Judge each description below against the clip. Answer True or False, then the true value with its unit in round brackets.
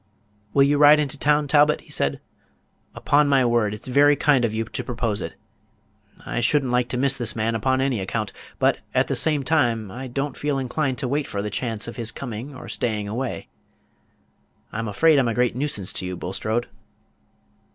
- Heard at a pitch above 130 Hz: False (125 Hz)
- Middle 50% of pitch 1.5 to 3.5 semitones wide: False (4.2 semitones)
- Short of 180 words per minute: False (205 wpm)